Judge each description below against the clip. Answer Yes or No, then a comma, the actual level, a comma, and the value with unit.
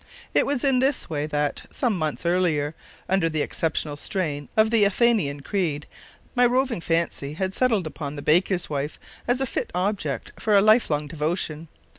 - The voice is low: No, medium, 170 Hz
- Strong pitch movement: Yes, wide, 6.4 semitones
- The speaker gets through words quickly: No, average, 175 wpm